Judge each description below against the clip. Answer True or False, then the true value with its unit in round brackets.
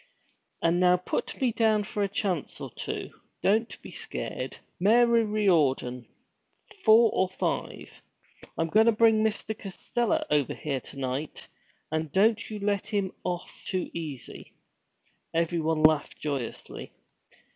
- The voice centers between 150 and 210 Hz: True (190 Hz)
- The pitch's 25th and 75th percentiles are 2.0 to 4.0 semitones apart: False (5.6 semitones)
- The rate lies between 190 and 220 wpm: False (135 wpm)